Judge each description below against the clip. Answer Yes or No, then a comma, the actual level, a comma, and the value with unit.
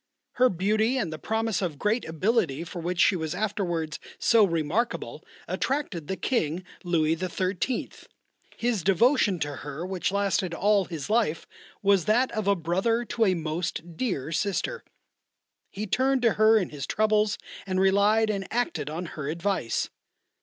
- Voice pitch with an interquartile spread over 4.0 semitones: Yes, average, 4.7 semitones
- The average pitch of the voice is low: No, high, 190 Hz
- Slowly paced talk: No, average, 155 wpm